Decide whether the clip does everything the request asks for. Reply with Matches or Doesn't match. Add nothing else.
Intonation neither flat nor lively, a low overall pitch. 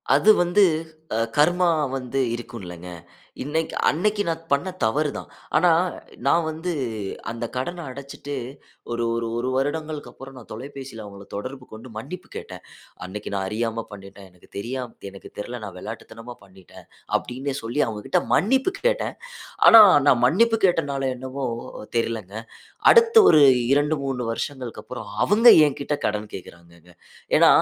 Doesn't match